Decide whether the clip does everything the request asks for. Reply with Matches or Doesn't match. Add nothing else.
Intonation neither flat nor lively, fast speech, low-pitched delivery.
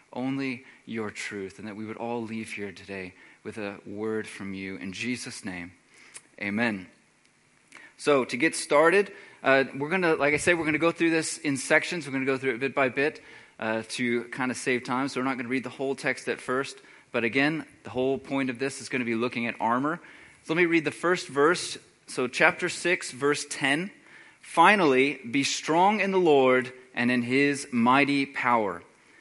Matches